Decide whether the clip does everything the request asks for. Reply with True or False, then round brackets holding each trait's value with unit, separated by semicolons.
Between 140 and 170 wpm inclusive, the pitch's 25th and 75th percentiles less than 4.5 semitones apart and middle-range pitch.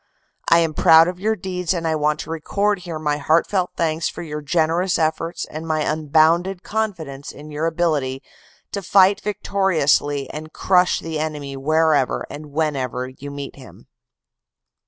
True (160 wpm; 3.1 semitones; 160 Hz)